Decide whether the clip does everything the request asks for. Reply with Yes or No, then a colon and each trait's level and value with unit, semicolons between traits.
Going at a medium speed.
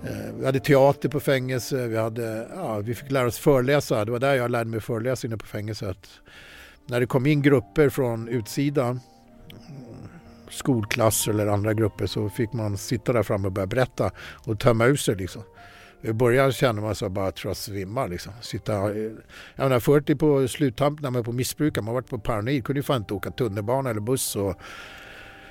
Yes: average, 185 wpm